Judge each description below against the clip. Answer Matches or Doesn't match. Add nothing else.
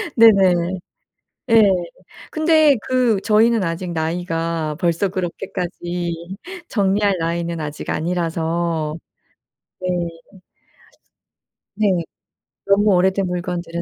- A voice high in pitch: Doesn't match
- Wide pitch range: Doesn't match